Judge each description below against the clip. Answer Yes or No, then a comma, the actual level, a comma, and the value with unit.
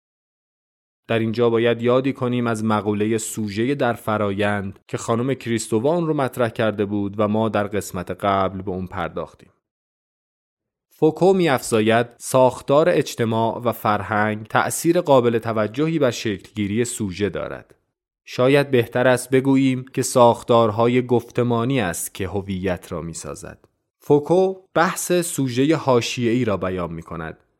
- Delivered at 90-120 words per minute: No, average, 130 wpm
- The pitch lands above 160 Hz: No, low, 115 Hz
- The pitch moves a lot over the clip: No, average, 3.5 semitones